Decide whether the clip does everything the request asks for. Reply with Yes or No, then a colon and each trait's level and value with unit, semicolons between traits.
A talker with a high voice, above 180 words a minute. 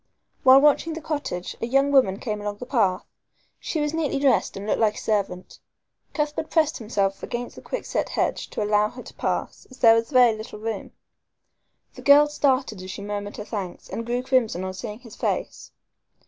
Yes: high, 230 Hz; average, 195 wpm